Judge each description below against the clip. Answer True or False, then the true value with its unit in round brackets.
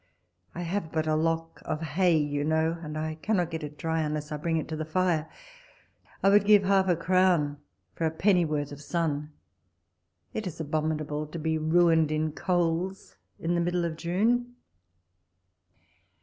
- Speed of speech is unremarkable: True (170 wpm)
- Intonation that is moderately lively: False (2.3 semitones)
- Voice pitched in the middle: True (165 Hz)